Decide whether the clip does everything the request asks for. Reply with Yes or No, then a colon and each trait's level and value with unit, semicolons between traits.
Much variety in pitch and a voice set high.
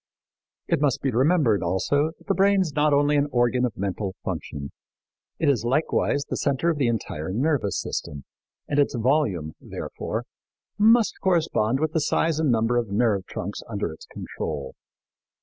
No: wide, 6.8 semitones; low, 130 Hz